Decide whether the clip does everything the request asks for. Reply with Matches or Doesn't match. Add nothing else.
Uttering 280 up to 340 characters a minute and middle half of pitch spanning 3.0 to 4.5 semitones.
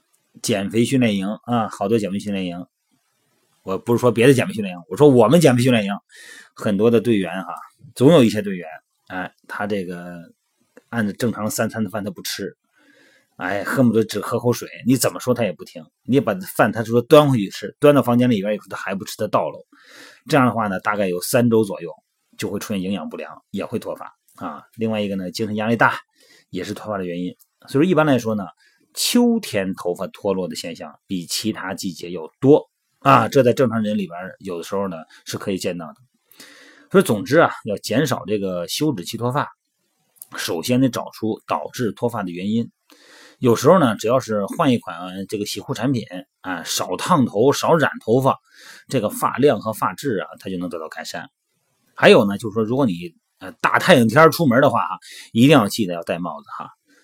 Matches